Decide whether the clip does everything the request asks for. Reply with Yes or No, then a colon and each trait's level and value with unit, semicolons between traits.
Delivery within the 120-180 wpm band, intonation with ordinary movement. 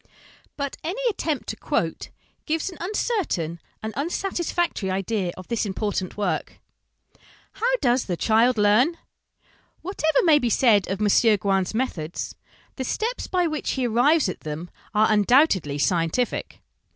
No: average, 140 wpm; wide, 8.4 semitones